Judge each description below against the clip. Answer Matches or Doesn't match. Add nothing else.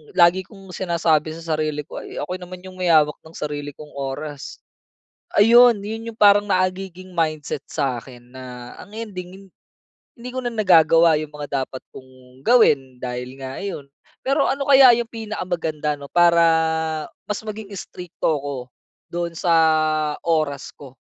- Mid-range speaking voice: Matches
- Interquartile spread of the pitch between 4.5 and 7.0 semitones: Matches